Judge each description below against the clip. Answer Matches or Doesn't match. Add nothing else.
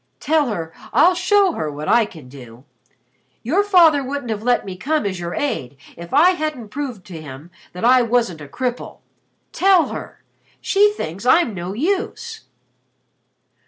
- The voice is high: Matches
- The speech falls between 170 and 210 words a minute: Doesn't match